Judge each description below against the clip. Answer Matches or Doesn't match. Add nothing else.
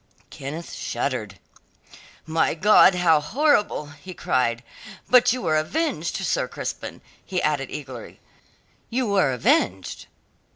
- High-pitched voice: Doesn't match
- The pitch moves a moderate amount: Doesn't match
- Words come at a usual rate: Doesn't match